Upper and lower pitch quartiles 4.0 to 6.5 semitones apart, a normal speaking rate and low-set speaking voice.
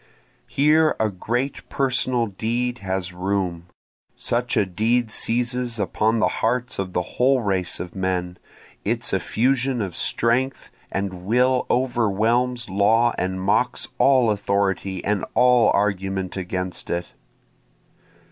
No: average, 4.5 semitones; slow, 120 wpm; low, 110 Hz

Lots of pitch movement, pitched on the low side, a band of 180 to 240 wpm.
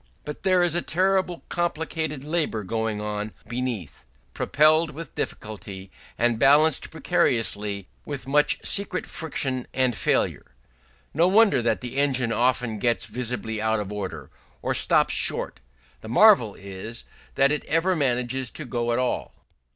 No: wide, 5.9 semitones; low, 125 Hz; average, 145 wpm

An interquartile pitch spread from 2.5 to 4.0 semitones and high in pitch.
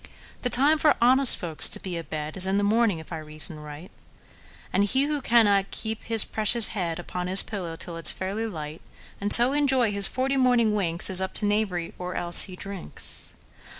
No: average, 5.3 semitones; high, 200 Hz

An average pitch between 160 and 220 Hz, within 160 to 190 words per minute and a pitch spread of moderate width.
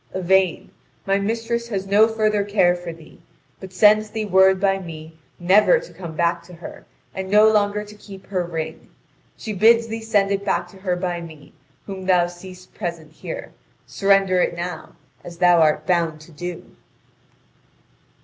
Yes: high, 190 Hz; average, 170 wpm; average, 3.1 semitones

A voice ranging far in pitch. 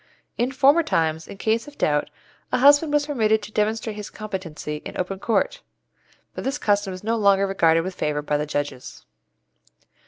Yes: wide, 6.0 semitones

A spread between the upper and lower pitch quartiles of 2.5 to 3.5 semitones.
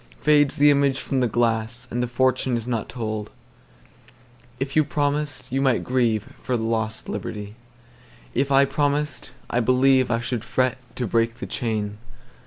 Yes: average, 3.0 semitones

